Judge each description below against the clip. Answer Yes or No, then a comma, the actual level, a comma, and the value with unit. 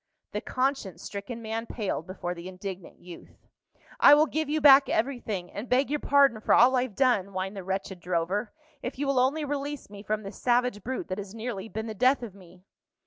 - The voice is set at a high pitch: Yes, high, 220 Hz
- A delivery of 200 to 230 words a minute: Yes, fast, 205 wpm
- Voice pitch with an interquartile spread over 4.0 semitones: Yes, wide, 5.4 semitones